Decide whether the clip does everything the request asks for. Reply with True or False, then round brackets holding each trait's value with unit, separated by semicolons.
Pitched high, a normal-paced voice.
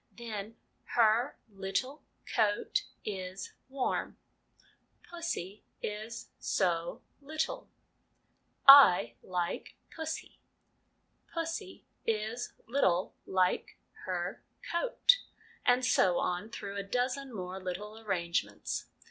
False (215 Hz; 100 wpm)